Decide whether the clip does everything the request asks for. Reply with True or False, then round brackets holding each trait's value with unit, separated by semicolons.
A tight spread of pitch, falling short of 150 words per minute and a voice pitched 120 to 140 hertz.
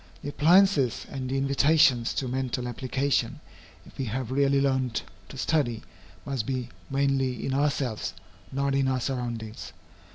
True (1.9 semitones; 140 wpm; 135 Hz)